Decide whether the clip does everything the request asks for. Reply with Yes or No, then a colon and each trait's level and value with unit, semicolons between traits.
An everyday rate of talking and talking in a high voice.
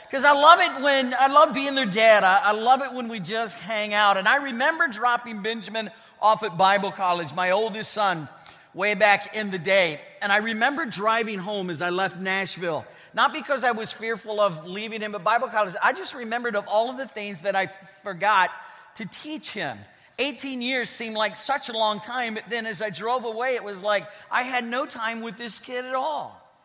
No: fast, 215 wpm; high, 220 Hz